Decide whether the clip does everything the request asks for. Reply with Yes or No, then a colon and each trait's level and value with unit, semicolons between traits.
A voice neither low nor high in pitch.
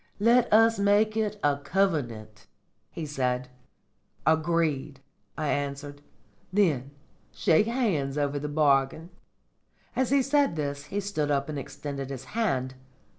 Yes: medium, 150 Hz